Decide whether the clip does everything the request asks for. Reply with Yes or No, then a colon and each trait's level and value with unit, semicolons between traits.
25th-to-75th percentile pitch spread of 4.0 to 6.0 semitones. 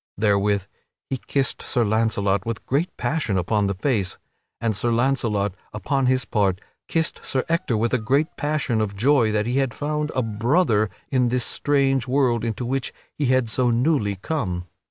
Yes: average, 4.3 semitones